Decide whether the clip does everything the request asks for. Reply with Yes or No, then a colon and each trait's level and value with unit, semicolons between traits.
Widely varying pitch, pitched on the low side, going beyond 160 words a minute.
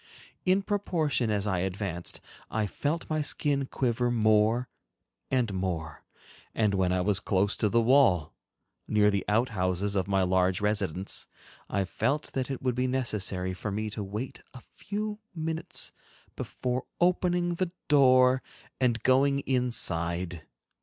No: wide, 5.7 semitones; low, 110 Hz; average, 140 wpm